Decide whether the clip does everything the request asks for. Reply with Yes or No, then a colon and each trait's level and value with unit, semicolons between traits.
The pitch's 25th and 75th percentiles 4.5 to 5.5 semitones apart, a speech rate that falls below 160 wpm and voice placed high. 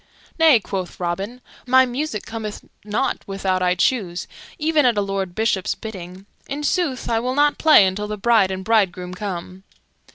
No: average, 4.9 semitones; average, 165 wpm; high, 210 Hz